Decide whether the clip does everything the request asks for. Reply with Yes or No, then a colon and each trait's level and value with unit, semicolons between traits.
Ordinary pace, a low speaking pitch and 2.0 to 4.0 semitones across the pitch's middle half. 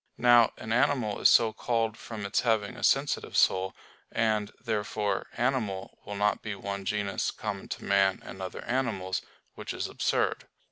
Yes: average, 160 wpm; low, 105 Hz; average, 2.9 semitones